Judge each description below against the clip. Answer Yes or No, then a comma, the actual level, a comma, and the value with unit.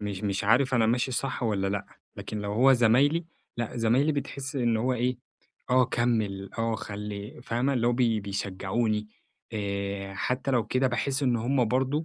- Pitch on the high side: No, low, 115 Hz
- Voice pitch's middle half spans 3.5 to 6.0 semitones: Yes, average, 3.8 semitones